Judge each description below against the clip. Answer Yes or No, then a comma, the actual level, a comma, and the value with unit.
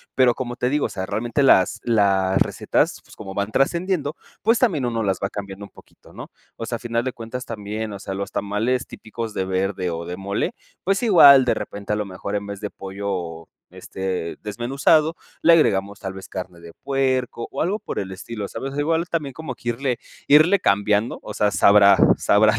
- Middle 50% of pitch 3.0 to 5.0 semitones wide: No, wide, 5.5 semitones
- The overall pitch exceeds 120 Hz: No, low, 110 Hz